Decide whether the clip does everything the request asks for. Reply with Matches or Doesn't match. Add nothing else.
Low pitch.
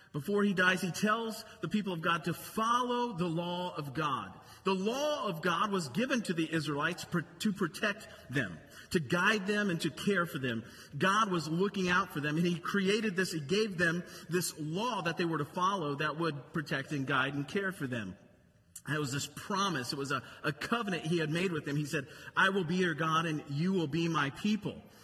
Doesn't match